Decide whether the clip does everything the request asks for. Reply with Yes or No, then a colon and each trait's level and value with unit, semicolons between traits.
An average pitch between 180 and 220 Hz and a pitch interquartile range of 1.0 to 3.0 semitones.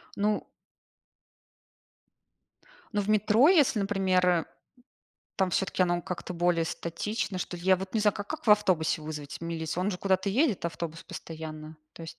No: medium, 185 Hz; average, 3.7 semitones